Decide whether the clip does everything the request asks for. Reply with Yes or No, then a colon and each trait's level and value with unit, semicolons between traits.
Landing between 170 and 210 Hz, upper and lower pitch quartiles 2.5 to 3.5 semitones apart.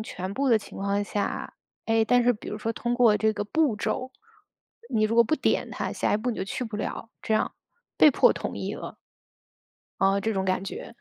No: high, 220 Hz; average, 2.8 semitones